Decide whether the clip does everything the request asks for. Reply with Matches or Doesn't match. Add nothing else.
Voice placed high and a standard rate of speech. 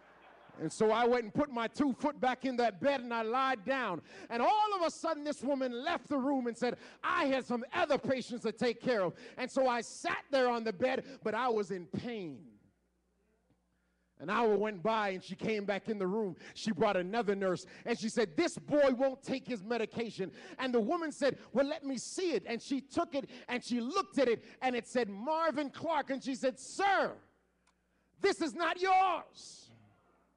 Doesn't match